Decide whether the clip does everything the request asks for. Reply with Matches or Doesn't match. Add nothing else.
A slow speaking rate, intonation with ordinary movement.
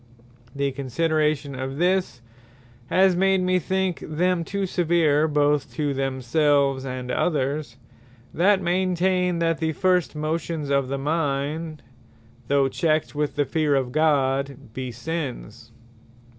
Matches